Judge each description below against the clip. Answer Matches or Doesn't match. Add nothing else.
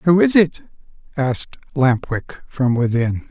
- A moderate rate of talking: Matches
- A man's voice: Matches